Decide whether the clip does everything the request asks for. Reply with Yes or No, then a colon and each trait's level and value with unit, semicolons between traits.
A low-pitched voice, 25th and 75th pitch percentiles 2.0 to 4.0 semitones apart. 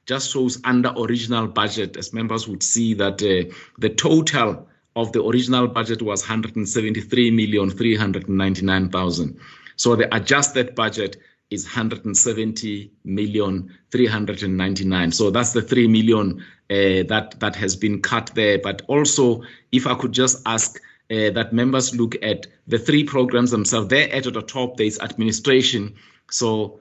Yes: low, 110 Hz; average, 3.0 semitones